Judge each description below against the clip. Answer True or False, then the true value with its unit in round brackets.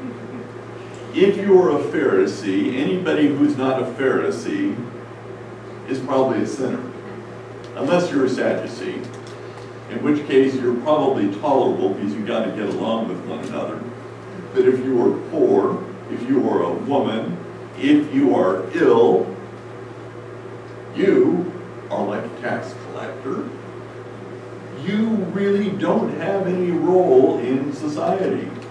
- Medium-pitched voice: True (170 Hz)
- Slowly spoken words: True (130 wpm)